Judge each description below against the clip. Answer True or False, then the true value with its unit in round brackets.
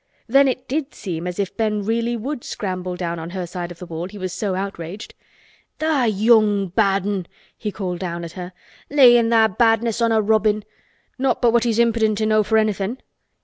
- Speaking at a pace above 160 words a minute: True (190 wpm)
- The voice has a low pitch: False (210 Hz)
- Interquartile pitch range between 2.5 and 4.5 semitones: True (4.0 semitones)